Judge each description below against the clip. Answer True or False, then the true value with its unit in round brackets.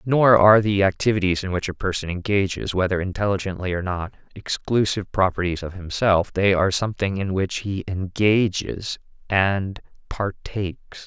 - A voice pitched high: False (95 Hz)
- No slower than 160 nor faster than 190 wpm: False (140 wpm)